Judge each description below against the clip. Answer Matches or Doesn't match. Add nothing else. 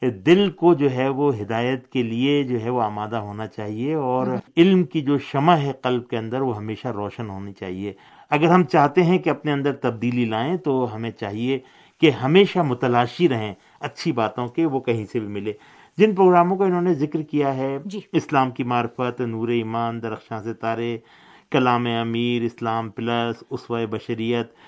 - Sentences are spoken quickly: Doesn't match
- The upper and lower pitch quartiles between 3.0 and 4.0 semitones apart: Doesn't match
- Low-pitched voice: Matches